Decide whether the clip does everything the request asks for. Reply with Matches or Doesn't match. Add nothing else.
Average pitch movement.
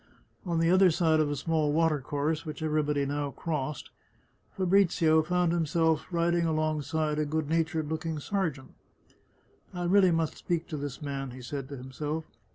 Doesn't match